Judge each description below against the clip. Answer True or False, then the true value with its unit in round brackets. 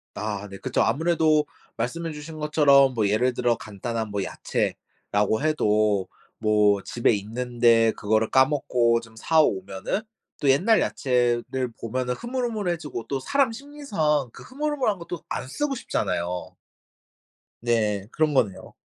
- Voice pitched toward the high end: False (125 Hz)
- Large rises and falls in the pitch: True (6.4 semitones)